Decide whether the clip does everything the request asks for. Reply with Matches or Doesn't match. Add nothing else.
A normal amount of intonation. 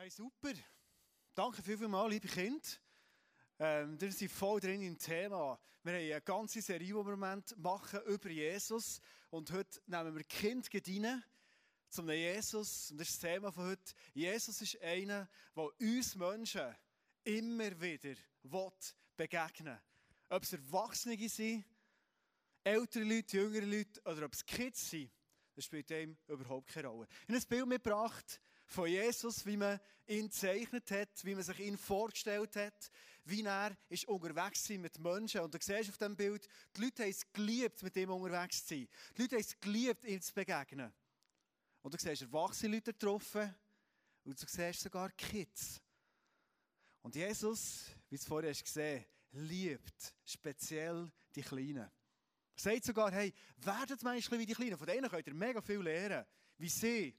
Matches